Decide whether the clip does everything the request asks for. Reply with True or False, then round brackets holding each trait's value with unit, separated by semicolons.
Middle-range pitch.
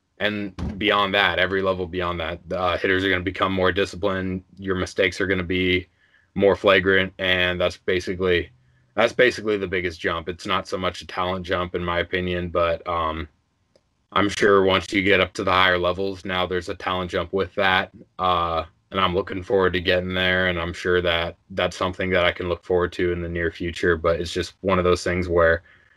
False (90 Hz)